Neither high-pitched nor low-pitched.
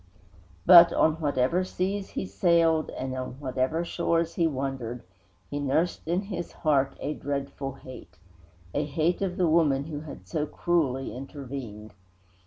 Yes: medium, 145 Hz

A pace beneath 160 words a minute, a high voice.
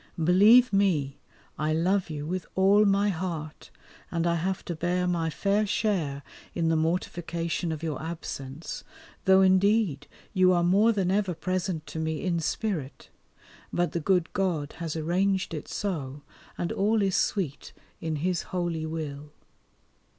No: average, 150 wpm; medium, 175 Hz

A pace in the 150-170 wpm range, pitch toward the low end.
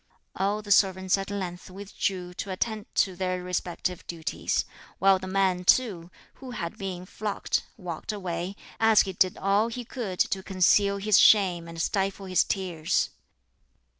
No: average, 155 wpm; high, 190 Hz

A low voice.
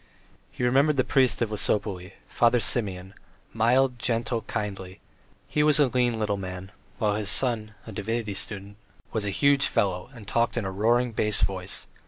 Yes: low, 110 Hz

